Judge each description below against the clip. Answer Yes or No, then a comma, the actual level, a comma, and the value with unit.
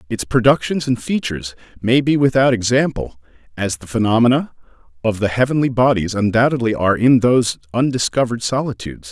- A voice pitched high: No, low, 115 Hz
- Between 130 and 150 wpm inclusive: Yes, average, 140 wpm